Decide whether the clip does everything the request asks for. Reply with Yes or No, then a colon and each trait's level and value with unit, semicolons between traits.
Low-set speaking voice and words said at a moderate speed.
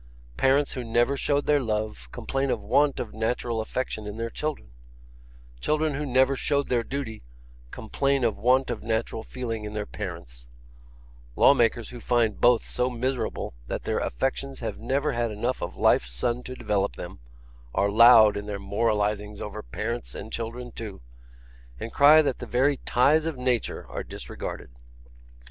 Yes: low, 120 Hz; average, 165 wpm